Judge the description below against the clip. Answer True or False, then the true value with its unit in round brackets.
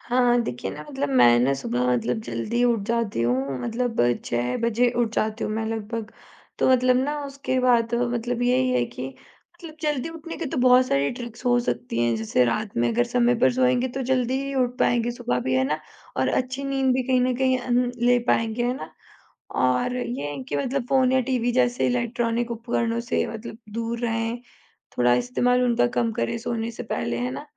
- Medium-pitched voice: False (235 Hz)